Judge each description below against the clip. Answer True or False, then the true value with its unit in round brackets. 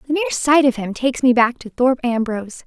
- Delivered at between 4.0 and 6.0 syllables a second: False (6.4 syllables/s)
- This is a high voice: True (255 Hz)